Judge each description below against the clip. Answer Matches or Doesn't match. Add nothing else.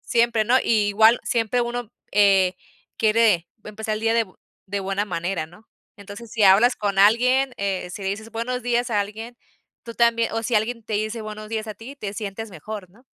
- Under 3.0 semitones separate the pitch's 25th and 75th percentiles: Matches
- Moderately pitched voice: Doesn't match